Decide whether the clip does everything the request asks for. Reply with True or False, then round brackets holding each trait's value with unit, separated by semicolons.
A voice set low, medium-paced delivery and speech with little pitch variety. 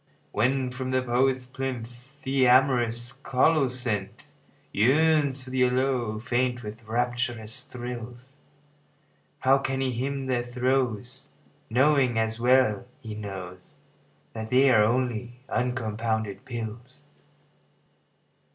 False (125 Hz; 105 wpm; 2.3 semitones)